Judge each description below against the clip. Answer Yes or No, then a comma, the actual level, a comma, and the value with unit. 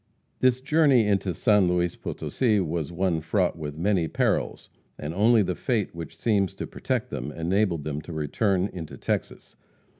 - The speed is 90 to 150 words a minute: No, average, 160 wpm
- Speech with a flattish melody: No, average, 4.3 semitones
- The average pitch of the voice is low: Yes, very low, 90 Hz